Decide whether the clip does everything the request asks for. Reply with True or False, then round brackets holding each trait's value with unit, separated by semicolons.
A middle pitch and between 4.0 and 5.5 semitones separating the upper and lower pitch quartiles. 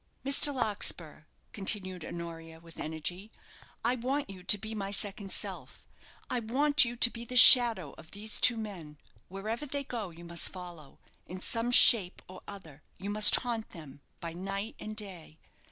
False (200 Hz; 5.2 semitones)